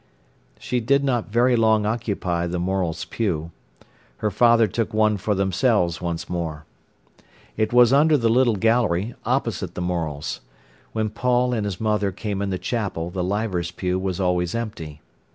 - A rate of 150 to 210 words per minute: Yes, average, 160 wpm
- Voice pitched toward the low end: Yes, low, 105 Hz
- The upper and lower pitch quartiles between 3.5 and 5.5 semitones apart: Yes, average, 4.5 semitones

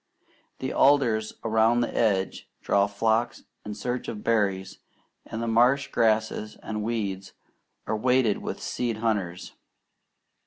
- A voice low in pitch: Yes, low, 110 Hz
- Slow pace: Yes, slow, 125 wpm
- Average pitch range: No, narrow, 2.1 semitones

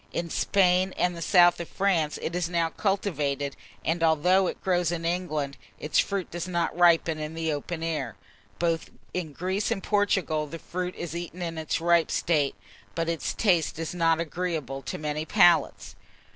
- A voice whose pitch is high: No, medium, 170 Hz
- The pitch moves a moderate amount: No, narrow, 2.1 semitones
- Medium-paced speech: Yes, average, 175 wpm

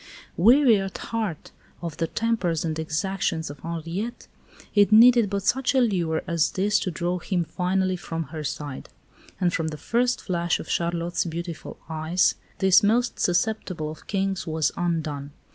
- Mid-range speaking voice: Yes, medium, 175 Hz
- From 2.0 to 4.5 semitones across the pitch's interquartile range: Yes, average, 3.9 semitones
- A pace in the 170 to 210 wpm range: No, average, 160 wpm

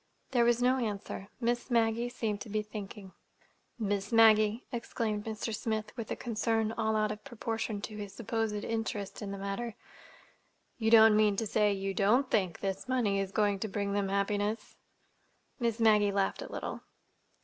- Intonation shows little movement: Yes, narrow, 2.0 semitones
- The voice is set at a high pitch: Yes, high, 215 Hz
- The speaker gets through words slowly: No, average, 170 wpm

